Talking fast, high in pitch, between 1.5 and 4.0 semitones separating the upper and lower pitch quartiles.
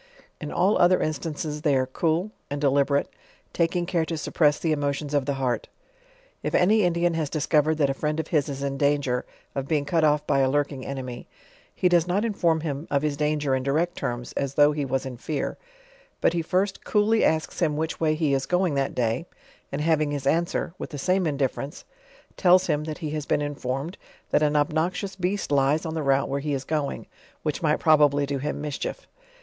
No: fast, 210 wpm; medium, 150 Hz; average, 2.9 semitones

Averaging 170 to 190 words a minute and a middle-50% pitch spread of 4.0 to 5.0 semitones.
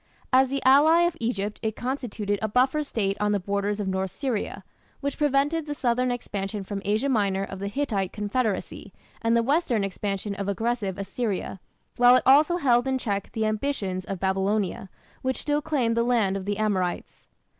Yes: average, 180 wpm; average, 4.7 semitones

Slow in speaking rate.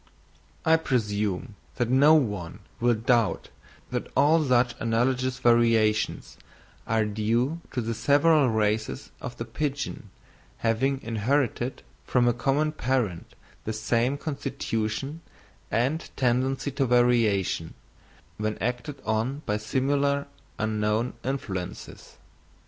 Yes: slow, 110 wpm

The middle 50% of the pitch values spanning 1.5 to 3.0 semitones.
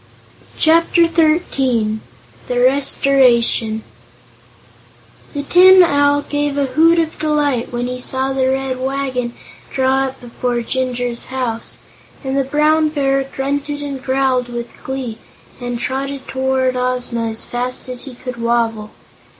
Yes: narrow, 2.5 semitones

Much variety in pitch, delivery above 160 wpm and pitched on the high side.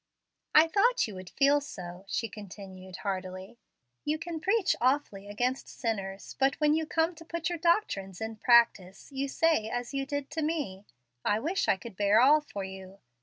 Yes: wide, 7.9 semitones; average, 180 wpm; high, 245 Hz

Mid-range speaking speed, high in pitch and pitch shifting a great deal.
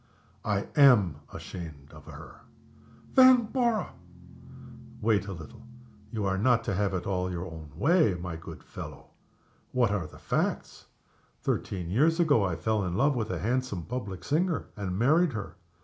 No: average, 155 wpm; low, 105 Hz; wide, 6.9 semitones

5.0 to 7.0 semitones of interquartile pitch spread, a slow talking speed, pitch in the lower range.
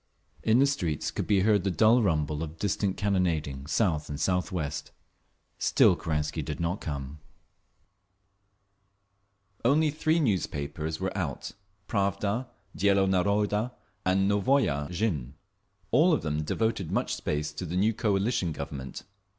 Yes: wide, 5.4 semitones; slow, 125 wpm; very low, 95 Hz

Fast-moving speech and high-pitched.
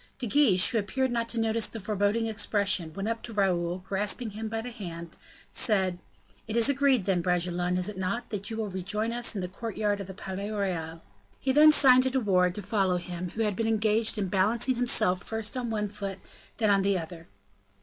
Yes: fast, 220 wpm; high, 205 Hz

